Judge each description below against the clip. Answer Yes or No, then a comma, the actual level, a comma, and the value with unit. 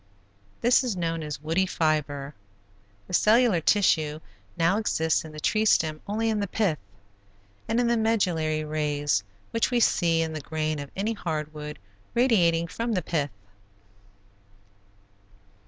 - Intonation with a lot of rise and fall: Yes, wide, 5.7 semitones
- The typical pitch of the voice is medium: Yes, medium, 165 Hz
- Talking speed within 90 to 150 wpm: Yes, average, 145 wpm